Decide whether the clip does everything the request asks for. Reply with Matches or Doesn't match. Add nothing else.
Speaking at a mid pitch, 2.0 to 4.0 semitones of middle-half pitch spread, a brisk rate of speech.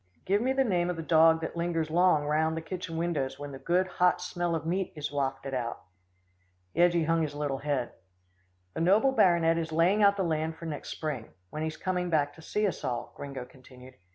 Matches